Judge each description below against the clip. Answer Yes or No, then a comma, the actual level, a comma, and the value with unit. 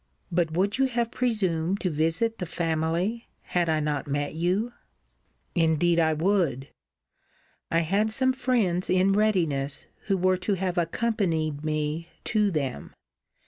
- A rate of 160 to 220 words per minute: No, average, 140 wpm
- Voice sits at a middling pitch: Yes, medium, 175 Hz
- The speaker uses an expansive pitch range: No, average, 4.5 semitones